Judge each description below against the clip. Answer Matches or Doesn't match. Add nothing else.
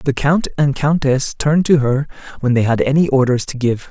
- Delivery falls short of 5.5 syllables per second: Matches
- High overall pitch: Doesn't match